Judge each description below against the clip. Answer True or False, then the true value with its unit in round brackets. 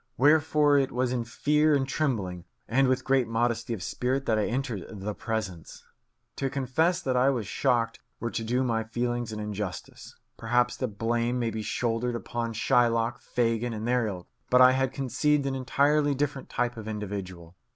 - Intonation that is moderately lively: True (3.0 semitones)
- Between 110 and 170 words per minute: False (180 wpm)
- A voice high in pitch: False (120 Hz)